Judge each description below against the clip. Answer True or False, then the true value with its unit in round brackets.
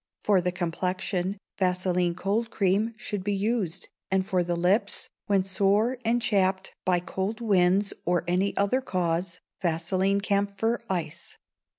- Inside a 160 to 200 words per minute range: False (135 wpm)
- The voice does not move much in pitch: True (2.2 semitones)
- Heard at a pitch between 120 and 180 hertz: False (190 Hz)